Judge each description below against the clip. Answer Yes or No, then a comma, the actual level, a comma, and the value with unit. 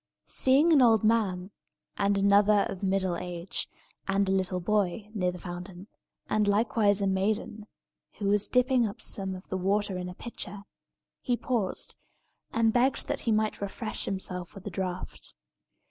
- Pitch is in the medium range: No, high, 200 Hz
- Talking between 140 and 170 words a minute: Yes, average, 160 wpm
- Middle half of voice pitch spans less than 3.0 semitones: Yes, narrow, 2.6 semitones